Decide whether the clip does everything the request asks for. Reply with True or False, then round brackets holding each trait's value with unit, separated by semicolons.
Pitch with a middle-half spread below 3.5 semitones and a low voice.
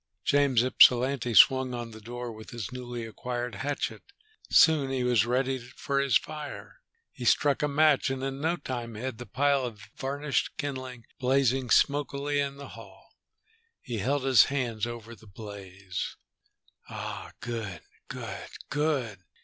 True (3.1 semitones; 125 Hz)